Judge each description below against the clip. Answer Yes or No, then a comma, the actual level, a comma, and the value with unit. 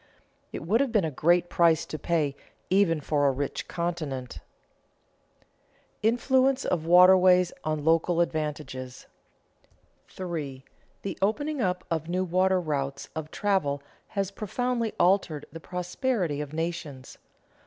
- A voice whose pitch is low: No, medium, 170 Hz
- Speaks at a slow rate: Yes, slow, 130 wpm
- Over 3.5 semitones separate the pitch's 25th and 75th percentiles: Yes, average, 4.1 semitones